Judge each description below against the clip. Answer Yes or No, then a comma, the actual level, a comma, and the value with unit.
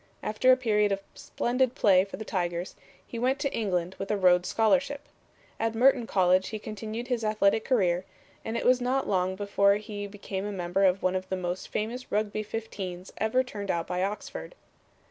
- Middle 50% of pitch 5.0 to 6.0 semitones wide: No, average, 3.7 semitones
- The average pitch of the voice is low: No, high, 210 Hz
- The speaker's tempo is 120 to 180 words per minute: No, average, 190 wpm